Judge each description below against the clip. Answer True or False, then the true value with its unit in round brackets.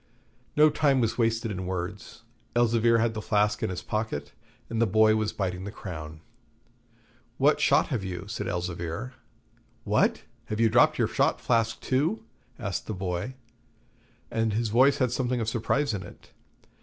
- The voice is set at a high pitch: False (110 Hz)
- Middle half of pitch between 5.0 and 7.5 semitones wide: False (3.9 semitones)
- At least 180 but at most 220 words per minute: False (165 wpm)